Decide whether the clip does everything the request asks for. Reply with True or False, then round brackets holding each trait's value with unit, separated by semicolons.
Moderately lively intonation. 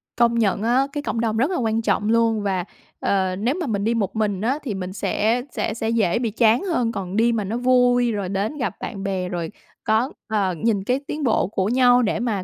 True (3.4 semitones)